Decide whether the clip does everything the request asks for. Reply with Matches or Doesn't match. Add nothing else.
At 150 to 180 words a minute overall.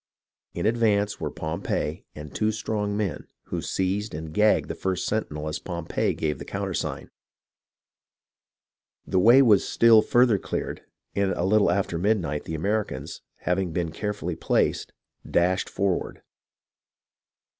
Doesn't match